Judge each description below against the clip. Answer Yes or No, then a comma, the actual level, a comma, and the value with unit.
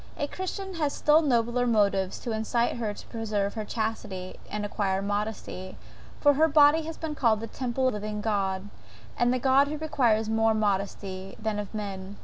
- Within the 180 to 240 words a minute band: Yes, average, 185 wpm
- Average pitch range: Yes, average, 4.3 semitones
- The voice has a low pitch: No, high, 220 Hz